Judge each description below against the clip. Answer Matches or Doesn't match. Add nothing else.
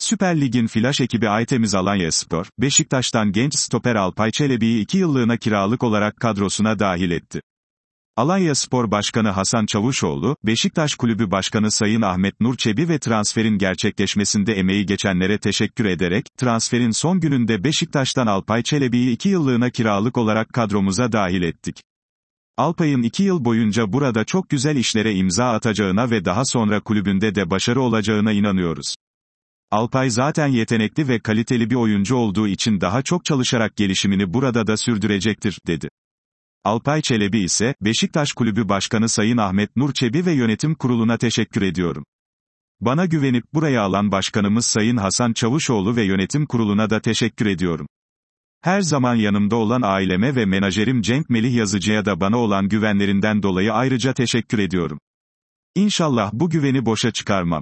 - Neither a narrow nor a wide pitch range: Matches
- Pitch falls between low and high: Doesn't match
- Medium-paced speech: Doesn't match